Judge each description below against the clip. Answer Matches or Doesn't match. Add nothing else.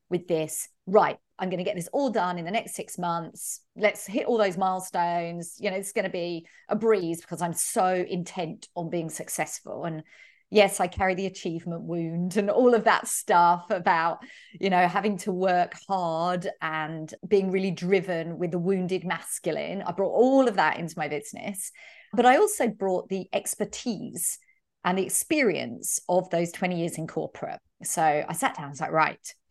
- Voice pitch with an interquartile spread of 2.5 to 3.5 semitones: Matches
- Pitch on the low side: Doesn't match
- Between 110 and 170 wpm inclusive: Doesn't match